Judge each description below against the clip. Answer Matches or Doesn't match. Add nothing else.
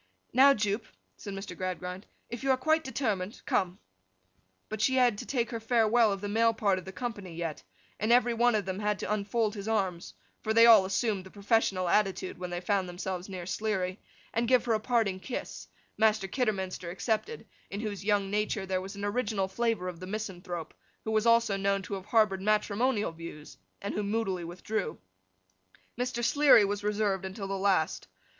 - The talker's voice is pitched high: Matches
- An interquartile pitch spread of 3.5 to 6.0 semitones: Doesn't match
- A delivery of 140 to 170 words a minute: Doesn't match